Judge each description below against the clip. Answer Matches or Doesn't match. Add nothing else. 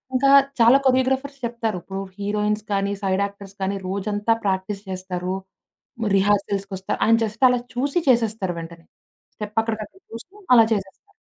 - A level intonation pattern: Doesn't match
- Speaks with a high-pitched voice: Matches